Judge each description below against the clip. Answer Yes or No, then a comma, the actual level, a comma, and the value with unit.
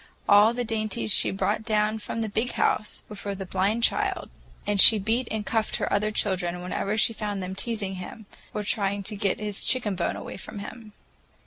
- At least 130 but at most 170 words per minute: No, fast, 205 wpm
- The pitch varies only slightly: Yes, narrow, 2.1 semitones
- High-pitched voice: Yes, high, 210 Hz